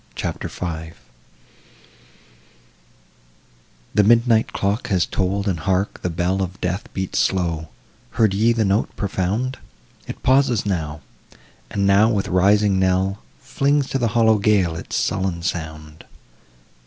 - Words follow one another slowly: Yes, slow, 130 wpm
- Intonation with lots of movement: No, average, 3.3 semitones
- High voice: No, very low, 95 Hz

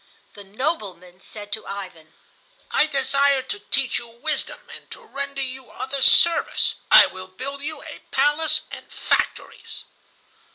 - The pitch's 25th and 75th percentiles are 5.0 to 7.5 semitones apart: Yes, wide, 5.6 semitones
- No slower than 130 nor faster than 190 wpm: Yes, average, 140 wpm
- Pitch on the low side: No, very high, 260 Hz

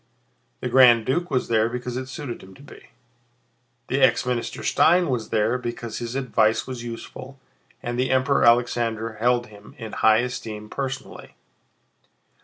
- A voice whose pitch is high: No, low, 120 Hz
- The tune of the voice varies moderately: No, narrow, 2.3 semitones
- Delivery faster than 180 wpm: No, average, 155 wpm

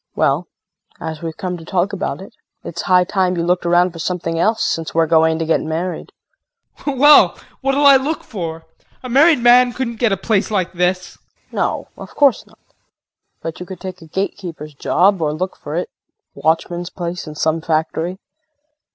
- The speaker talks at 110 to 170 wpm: No, average, 185 wpm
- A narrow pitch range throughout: No, average, 3.9 semitones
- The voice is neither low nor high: Yes, medium, 180 Hz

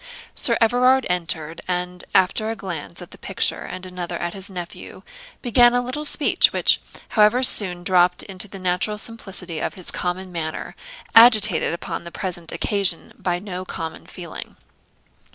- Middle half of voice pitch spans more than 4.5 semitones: No, average, 3.5 semitones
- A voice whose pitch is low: No, medium, 185 Hz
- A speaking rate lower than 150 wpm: No, average, 155 wpm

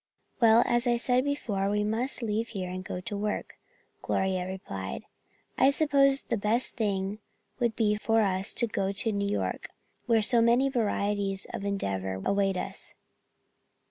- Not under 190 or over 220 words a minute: No, average, 160 wpm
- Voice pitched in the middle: No, high, 210 Hz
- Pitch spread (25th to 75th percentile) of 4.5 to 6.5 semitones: No, average, 3.3 semitones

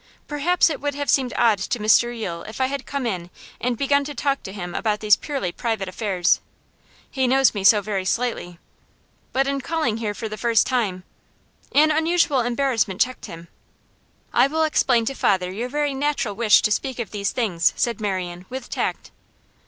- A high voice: Yes, high, 235 Hz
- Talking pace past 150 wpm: Yes, average, 190 wpm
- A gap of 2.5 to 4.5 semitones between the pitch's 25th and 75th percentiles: No, average, 5.3 semitones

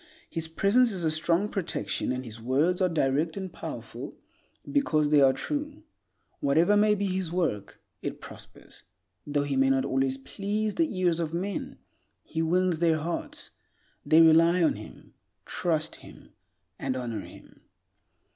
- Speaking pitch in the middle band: Yes, medium, 165 Hz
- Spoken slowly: No, average, 150 wpm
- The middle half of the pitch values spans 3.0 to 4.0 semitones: No, average, 5.2 semitones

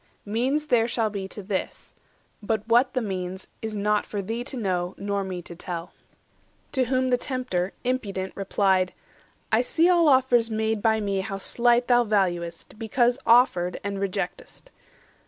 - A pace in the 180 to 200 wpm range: No, average, 160 wpm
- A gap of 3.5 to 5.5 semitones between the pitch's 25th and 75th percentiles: Yes, average, 4.2 semitones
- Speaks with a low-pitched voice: No, high, 215 Hz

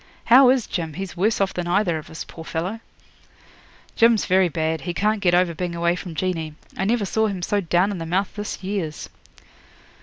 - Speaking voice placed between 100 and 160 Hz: No, medium, 185 Hz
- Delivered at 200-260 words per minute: Yes, fast, 205 wpm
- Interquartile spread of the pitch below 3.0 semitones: No, average, 3.3 semitones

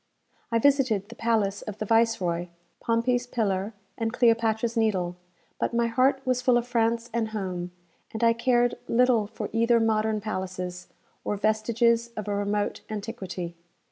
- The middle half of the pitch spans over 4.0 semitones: No, narrow, 2.4 semitones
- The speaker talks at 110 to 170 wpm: Yes, average, 150 wpm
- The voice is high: Yes, high, 225 Hz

